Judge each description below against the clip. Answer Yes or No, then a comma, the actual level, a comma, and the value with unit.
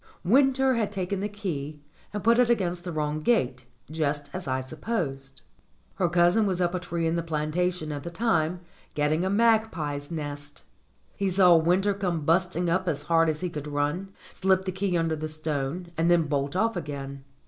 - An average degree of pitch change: Yes, average, 4.1 semitones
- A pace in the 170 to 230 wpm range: Yes, average, 190 wpm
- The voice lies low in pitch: No, medium, 170 Hz